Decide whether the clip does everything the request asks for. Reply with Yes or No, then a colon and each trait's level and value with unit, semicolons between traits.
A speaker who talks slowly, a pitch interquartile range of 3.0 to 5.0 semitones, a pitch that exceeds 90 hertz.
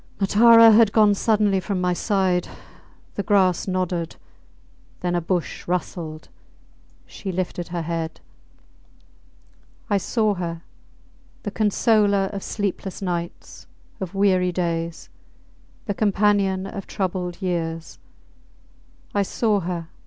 No: slow, 110 wpm; narrow, 2.6 semitones; high, 190 Hz